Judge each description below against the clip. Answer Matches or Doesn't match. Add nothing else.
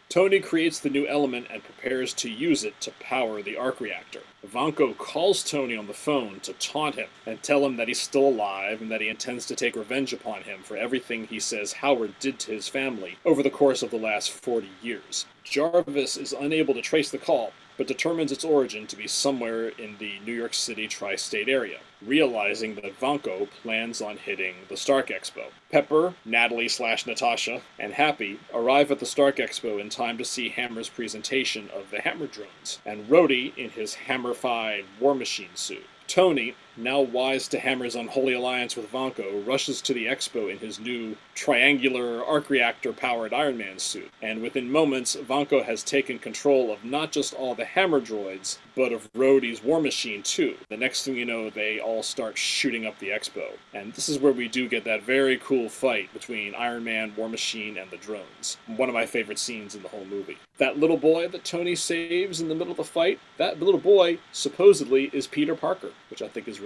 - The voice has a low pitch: Matches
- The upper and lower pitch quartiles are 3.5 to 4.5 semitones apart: Matches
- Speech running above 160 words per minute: Matches